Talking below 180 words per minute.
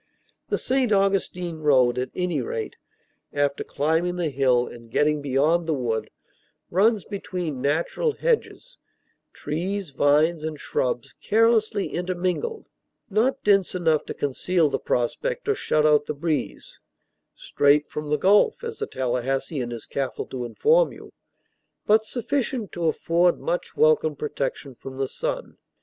Yes: average, 140 wpm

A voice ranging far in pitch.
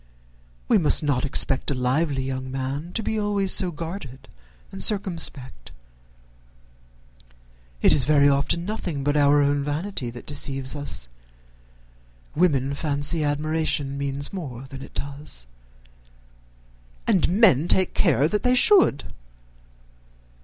No: average, 4.0 semitones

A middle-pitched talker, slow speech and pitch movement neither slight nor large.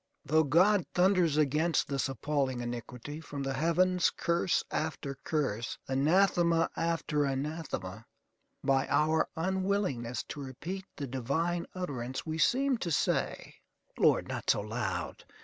Yes: medium, 150 Hz; slow, 125 wpm; average, 4.4 semitones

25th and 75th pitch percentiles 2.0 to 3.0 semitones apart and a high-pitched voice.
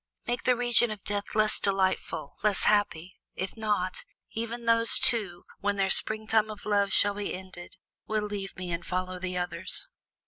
Yes: narrow, 2.6 semitones; high, 205 Hz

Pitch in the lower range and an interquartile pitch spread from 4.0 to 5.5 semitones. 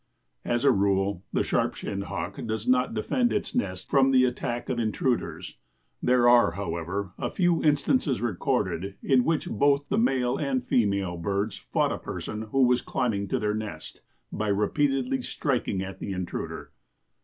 Yes: low, 115 Hz; average, 5.1 semitones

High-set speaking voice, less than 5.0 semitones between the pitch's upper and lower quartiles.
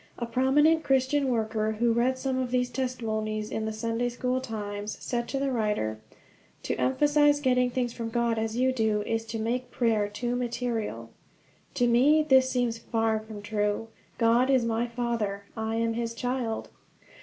Yes: high, 235 Hz; narrow, 2.5 semitones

